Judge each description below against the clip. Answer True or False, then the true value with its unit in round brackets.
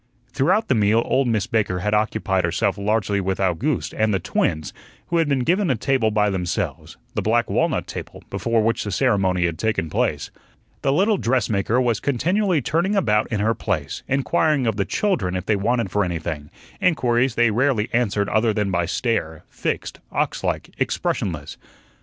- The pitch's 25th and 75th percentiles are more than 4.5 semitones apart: True (5.0 semitones)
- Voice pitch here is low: True (110 Hz)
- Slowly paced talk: False (175 wpm)